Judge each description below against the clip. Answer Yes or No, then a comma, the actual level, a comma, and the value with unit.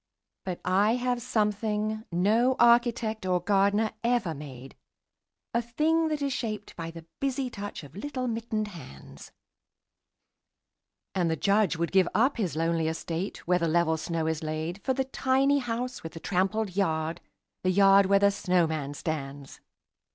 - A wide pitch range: Yes, wide, 6.0 semitones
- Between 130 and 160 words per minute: Yes, average, 155 wpm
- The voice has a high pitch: Yes, high, 200 Hz